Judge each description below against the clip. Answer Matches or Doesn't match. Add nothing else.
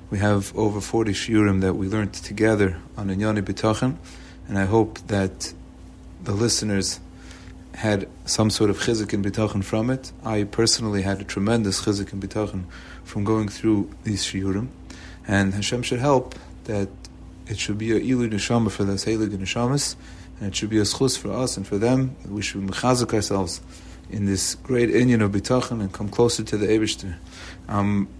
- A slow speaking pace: Doesn't match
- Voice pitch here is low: Matches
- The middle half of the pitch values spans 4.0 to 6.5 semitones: Doesn't match